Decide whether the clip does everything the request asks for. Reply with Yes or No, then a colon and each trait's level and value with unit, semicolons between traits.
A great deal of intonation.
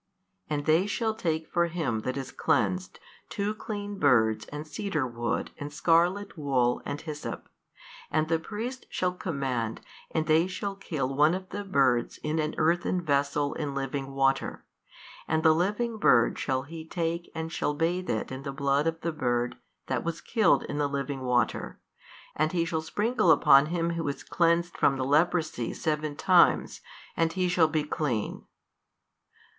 No: average, 3.9 semitones